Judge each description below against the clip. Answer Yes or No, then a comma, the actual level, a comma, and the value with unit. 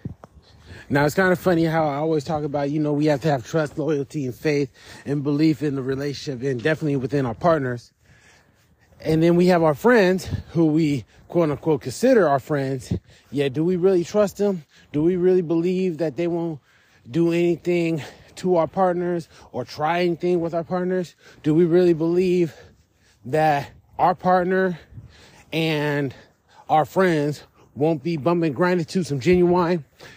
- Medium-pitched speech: Yes, medium, 155 Hz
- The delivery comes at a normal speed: Yes, average, 165 wpm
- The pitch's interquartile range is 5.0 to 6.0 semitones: No, average, 3.7 semitones